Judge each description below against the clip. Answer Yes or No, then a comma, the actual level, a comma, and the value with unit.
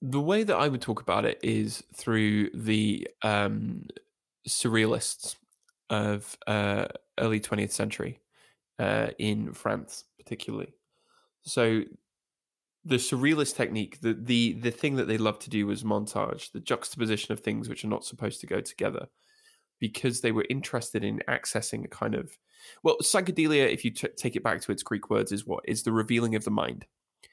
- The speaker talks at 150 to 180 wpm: Yes, average, 170 wpm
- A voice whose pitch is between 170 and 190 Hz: No, low, 115 Hz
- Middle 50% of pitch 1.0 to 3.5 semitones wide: No, average, 4.4 semitones